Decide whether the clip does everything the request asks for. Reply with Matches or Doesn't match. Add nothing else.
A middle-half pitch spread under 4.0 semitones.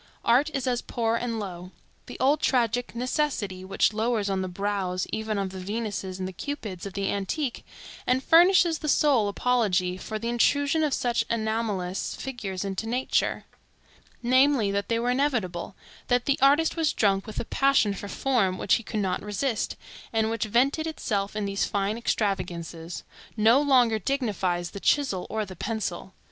Doesn't match